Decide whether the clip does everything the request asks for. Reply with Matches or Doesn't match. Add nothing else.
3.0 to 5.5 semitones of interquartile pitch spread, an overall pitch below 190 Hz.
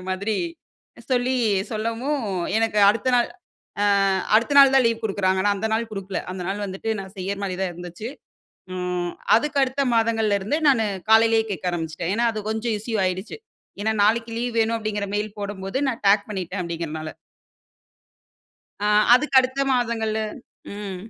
Doesn't match